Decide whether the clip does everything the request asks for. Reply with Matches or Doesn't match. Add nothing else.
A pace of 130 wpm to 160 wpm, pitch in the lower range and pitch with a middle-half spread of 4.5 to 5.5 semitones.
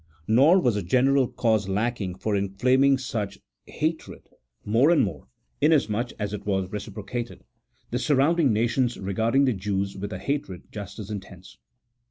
Matches